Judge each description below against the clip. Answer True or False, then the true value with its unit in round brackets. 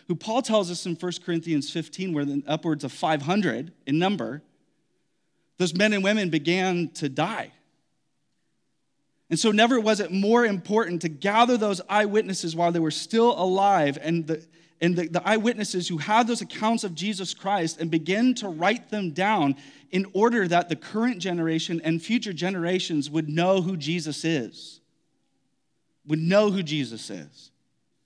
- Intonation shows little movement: False (4.2 semitones)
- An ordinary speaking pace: True (165 wpm)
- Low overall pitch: False (180 Hz)